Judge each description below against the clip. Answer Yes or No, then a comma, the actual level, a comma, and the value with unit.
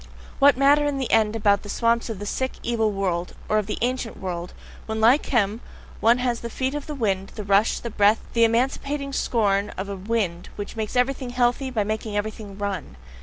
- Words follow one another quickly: Yes, fast, 210 wpm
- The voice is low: No, high, 225 Hz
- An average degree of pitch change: Yes, average, 3.6 semitones